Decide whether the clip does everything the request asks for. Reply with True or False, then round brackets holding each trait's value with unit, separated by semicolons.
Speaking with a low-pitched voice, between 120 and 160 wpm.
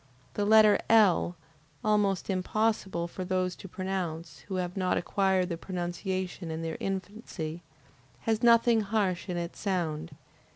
False (185 Hz; 135 wpm)